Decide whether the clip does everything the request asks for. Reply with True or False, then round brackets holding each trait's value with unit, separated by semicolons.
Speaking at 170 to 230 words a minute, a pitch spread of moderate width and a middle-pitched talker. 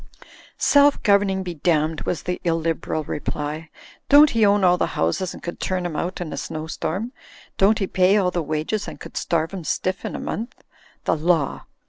True (200 wpm; 3.7 semitones; 180 Hz)